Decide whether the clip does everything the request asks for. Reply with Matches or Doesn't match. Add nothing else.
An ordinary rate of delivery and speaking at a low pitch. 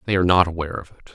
Doesn't match